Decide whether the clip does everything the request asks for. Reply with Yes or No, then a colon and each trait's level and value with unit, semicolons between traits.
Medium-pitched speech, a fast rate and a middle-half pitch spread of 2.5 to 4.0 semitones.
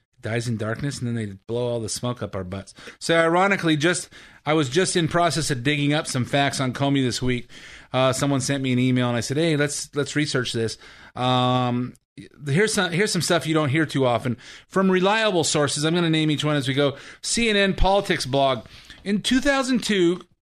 No: medium, 145 Hz; fast, 210 wpm; wide, 5.6 semitones